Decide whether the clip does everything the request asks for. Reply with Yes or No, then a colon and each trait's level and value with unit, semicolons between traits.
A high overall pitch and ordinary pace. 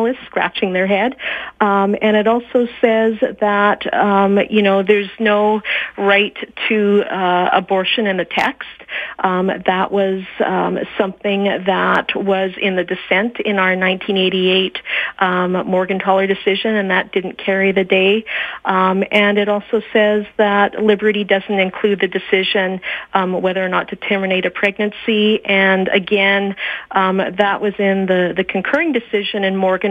Yes: high, 200 Hz; average, 150 wpm